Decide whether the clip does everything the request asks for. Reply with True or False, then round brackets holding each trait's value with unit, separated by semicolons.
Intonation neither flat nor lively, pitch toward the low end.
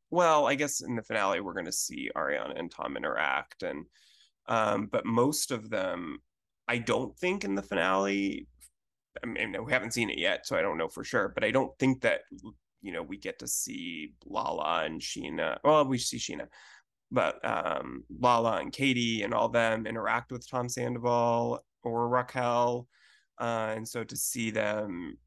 True (4.1 semitones; 120 Hz)